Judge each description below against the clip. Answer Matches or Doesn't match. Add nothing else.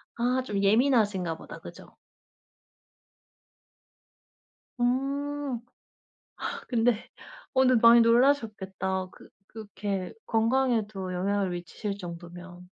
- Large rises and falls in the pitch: Doesn't match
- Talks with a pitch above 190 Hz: Matches